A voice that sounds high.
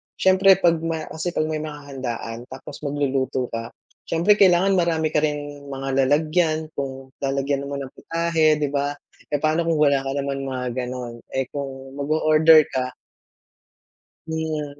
No: medium, 145 Hz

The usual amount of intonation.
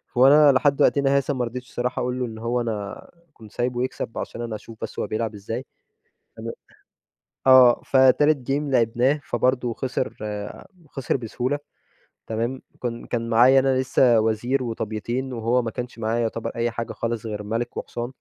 No: narrow, 2.3 semitones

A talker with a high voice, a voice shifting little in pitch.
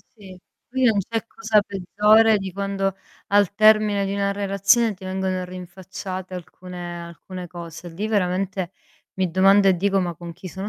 Yes: high, 195 Hz; narrow, 2.0 semitones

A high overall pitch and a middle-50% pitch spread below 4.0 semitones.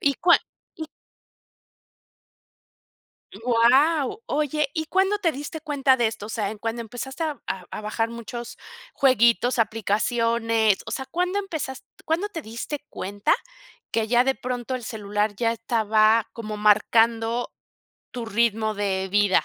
No: high, 235 Hz; average, 4.3 semitones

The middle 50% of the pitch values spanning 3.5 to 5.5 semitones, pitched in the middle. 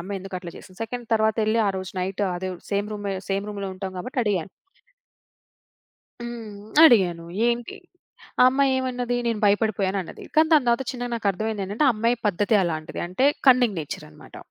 No: average, 4.0 semitones; high, 210 Hz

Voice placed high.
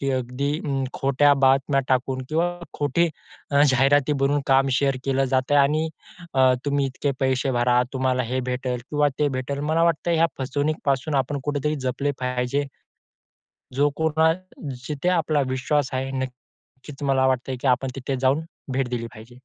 No: low, 135 Hz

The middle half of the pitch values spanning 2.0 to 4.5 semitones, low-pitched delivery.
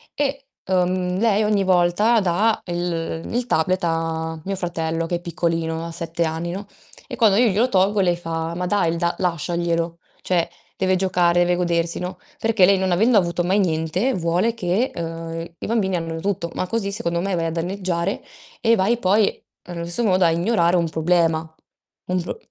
No: average, 2.7 semitones; medium, 175 Hz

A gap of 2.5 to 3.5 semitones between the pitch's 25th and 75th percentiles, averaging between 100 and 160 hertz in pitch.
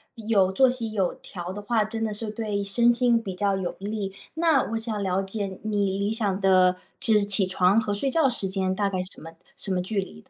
No: average, 2.8 semitones; high, 205 Hz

